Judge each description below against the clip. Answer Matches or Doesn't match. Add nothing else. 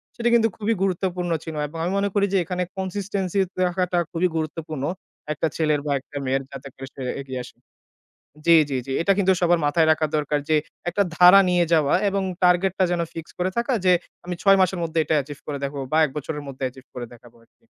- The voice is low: Doesn't match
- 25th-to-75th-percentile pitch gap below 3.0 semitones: Doesn't match